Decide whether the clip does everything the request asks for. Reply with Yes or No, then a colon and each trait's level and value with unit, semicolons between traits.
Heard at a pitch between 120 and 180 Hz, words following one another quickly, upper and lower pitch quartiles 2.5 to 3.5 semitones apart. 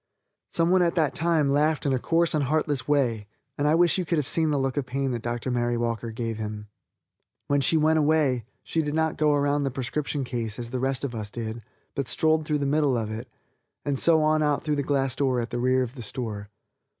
No: medium, 140 Hz; fast, 240 wpm; average, 4.2 semitones